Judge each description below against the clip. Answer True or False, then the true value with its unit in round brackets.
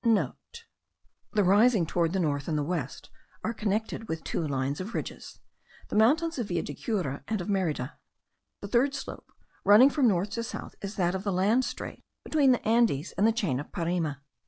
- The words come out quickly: False (190 wpm)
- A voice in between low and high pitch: False (200 Hz)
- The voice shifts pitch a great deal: True (5.7 semitones)